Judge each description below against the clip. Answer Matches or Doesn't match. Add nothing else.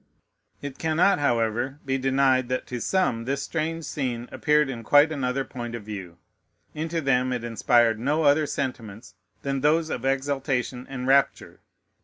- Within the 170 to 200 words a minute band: Doesn't match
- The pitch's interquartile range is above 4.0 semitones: Doesn't match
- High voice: Doesn't match